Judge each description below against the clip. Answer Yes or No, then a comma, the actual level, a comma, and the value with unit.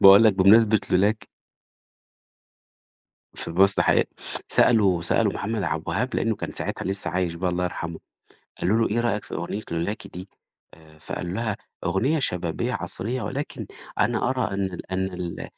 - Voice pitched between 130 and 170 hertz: No, very low, 95 Hz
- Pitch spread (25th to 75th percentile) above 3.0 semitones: Yes, average, 3.7 semitones